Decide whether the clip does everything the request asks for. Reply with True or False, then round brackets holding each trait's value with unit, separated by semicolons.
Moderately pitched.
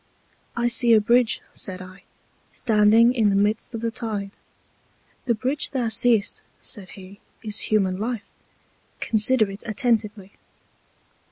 False (215 Hz)